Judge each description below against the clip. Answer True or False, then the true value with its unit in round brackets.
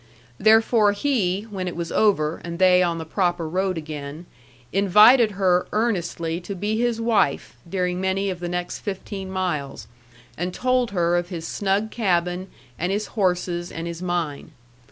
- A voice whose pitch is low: False (185 Hz)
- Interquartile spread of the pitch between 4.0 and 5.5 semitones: False (2.9 semitones)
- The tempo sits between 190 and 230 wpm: False (160 wpm)